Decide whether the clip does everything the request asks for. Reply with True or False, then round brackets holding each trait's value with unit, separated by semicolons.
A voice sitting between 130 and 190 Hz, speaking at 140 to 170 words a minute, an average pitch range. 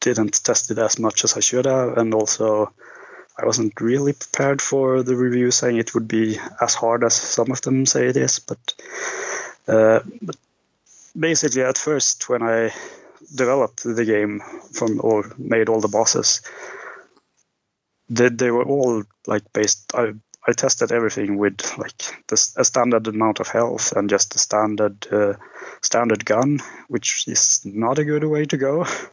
False (115 Hz; 165 wpm; 3.1 semitones)